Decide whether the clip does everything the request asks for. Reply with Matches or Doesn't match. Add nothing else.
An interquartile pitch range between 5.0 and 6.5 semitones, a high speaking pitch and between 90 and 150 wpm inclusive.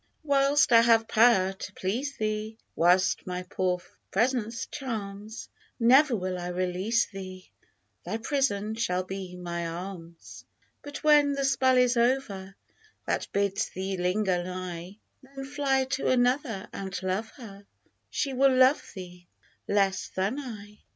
Matches